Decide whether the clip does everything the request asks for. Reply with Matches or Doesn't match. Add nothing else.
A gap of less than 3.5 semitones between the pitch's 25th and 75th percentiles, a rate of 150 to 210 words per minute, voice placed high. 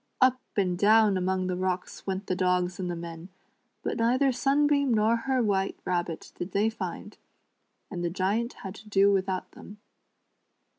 Doesn't match